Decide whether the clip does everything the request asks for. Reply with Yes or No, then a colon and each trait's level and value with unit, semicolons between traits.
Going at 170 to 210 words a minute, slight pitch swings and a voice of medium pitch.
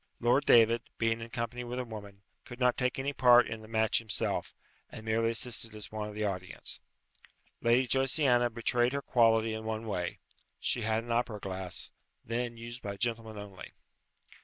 No: average, 180 wpm; narrow, 1.9 semitones; low, 115 Hz